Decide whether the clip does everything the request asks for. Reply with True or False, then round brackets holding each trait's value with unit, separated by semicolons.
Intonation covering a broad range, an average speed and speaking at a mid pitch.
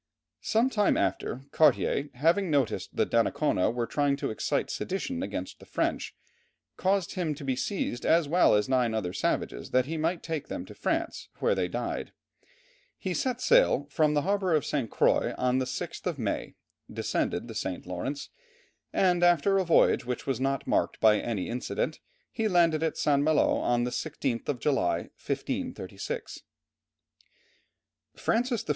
True (6.3 semitones; 165 wpm; 150 Hz)